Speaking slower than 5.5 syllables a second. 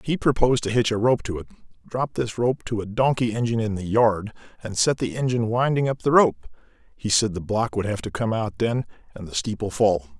No: 5.7 syllables/s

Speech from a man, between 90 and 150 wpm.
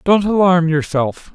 Yes: male; slow, 135 wpm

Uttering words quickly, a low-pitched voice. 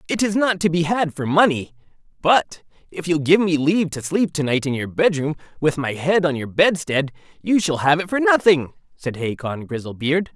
No: fast, 210 wpm; medium, 160 Hz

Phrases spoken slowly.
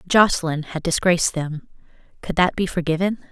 No: average, 145 wpm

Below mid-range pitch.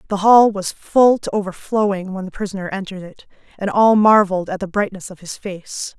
No: high, 195 Hz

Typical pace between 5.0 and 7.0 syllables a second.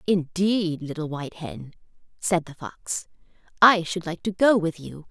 No: 4.3 syllables/s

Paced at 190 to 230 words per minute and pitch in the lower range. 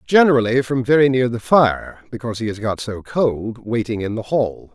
Yes: average, 200 wpm; low, 120 Hz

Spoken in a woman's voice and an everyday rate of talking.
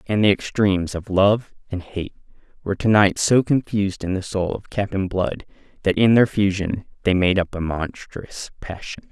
No: male; average, 185 wpm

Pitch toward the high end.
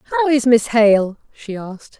Yes: high, 225 Hz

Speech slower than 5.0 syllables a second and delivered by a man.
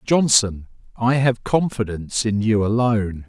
Yes: 4.5 syllables/s; male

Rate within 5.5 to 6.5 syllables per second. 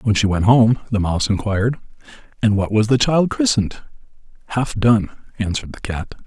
Yes: 5.7 syllables/s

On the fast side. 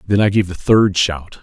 Yes: fast, 255 wpm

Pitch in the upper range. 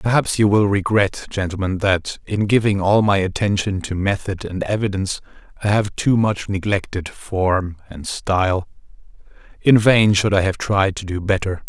No: low, 100 Hz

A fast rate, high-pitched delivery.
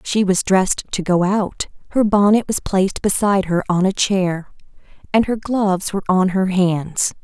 No: average, 185 wpm; high, 195 Hz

